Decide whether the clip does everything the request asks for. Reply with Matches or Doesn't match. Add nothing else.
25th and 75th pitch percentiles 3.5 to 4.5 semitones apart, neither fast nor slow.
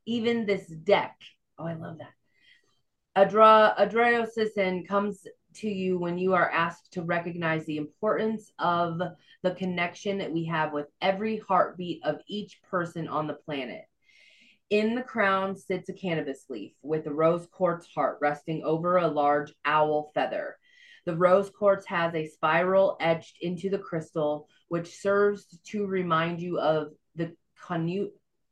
Matches